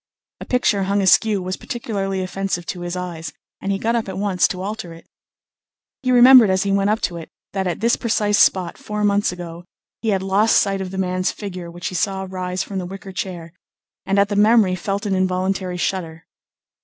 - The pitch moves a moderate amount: No, narrow, 2.0 semitones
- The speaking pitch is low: No, high, 190 Hz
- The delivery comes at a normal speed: No, fast, 210 wpm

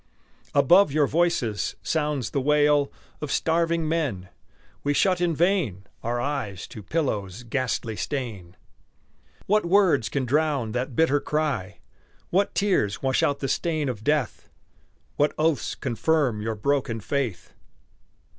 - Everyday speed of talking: No, slow, 130 wpm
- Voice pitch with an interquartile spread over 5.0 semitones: Yes, wide, 5.6 semitones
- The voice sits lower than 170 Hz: Yes, medium, 140 Hz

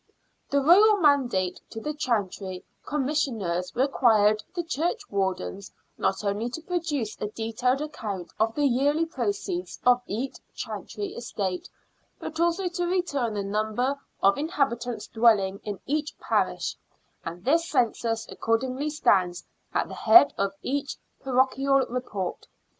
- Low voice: No, very high, 250 Hz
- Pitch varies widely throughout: Yes, wide, 6.2 semitones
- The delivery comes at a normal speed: No, slow, 130 wpm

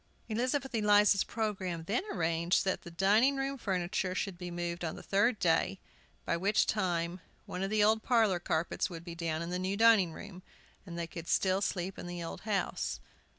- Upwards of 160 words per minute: Yes, average, 190 wpm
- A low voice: No, medium, 185 Hz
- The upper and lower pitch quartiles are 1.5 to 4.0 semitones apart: Yes, average, 3.5 semitones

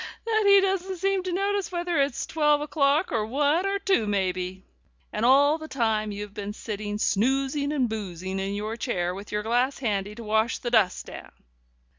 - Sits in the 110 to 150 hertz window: No, high, 240 Hz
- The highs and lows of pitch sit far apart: Yes, wide, 7.1 semitones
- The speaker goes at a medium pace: Yes, average, 185 wpm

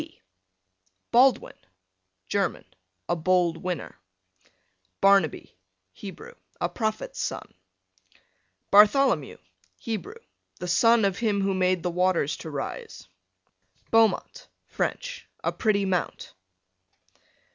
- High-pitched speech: Yes, high, 195 Hz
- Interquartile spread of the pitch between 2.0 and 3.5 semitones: No, average, 4.3 semitones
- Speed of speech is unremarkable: No, slow, 95 wpm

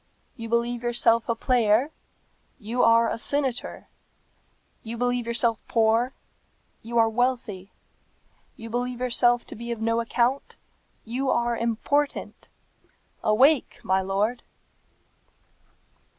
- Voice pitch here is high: Yes, high, 235 Hz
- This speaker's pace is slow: Yes, slow, 110 wpm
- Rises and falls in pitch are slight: Yes, narrow, 1.4 semitones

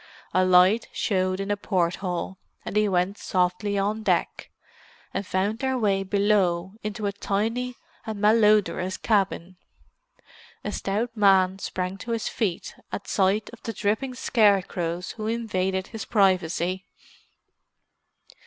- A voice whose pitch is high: Yes, high, 200 Hz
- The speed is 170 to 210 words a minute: No, slow, 135 wpm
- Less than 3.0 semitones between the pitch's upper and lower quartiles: Yes, narrow, 2.4 semitones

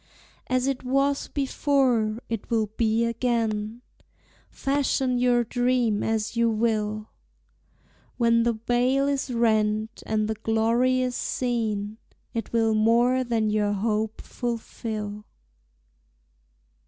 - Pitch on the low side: No, high, 230 Hz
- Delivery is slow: Yes, slow, 110 wpm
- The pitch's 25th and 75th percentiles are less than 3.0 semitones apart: Yes, narrow, 2.4 semitones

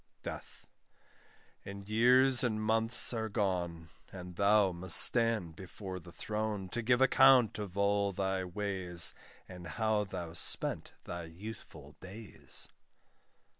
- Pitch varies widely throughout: No, average, 3.5 semitones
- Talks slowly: Yes, slow, 125 wpm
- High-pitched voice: No, low, 100 Hz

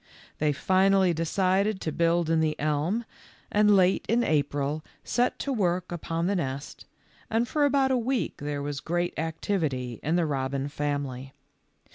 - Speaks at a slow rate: No, average, 155 wpm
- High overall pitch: No, medium, 165 Hz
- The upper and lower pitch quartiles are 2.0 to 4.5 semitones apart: No, average, 5.2 semitones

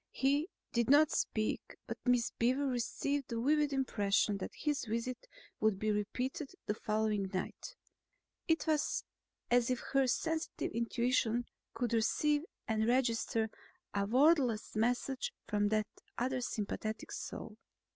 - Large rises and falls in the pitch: No, average, 3.9 semitones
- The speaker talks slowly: Yes, slow, 130 wpm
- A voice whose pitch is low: No, high, 240 Hz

